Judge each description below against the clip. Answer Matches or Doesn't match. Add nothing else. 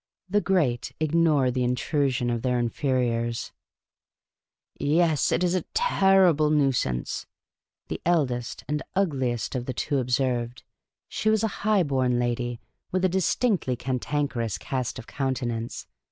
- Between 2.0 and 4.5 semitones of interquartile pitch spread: Doesn't match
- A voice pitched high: Doesn't match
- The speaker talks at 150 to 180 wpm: Doesn't match